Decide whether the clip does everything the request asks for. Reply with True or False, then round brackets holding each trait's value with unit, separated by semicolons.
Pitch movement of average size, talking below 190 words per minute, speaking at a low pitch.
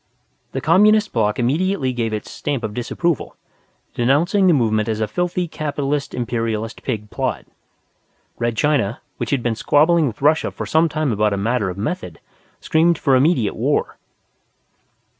False (6.0 semitones; 155 wpm; 130 Hz)